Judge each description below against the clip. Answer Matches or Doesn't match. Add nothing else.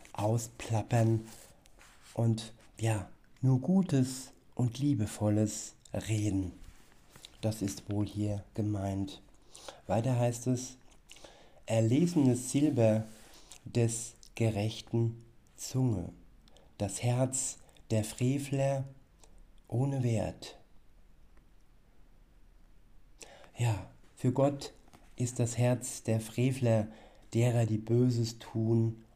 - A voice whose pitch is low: Matches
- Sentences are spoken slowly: Matches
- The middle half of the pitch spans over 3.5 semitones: Doesn't match